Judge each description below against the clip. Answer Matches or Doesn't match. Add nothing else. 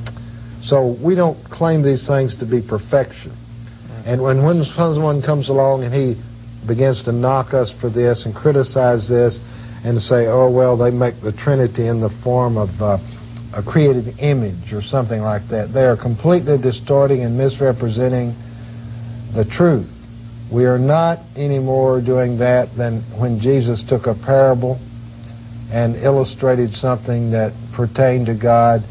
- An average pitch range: Doesn't match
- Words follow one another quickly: Doesn't match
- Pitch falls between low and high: Doesn't match